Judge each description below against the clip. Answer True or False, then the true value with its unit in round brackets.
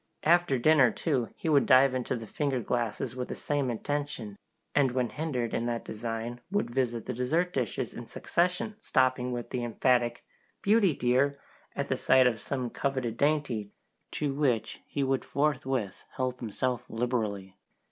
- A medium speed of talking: True (160 wpm)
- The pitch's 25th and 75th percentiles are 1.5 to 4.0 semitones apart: True (3.2 semitones)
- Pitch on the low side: True (130 Hz)